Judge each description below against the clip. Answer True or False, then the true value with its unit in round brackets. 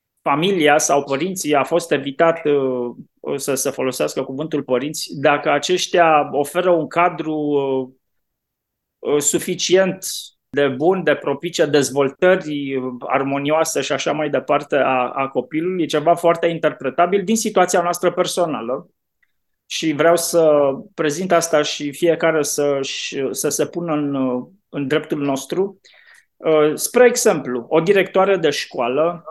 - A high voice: False (155 Hz)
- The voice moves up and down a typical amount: True (3.7 semitones)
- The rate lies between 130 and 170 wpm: False (120 wpm)